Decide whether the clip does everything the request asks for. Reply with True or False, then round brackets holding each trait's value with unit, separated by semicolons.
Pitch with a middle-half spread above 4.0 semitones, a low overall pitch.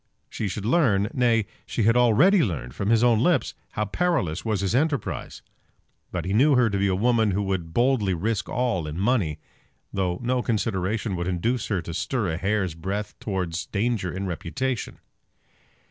True (4.7 semitones; 105 Hz)